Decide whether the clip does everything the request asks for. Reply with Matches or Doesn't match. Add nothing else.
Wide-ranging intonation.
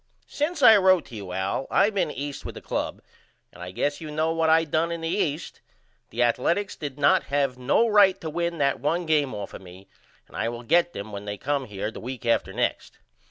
Matches